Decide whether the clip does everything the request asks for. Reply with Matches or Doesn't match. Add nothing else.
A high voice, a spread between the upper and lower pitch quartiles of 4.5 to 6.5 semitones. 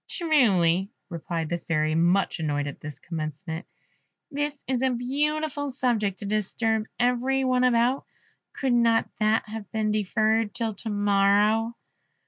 Matches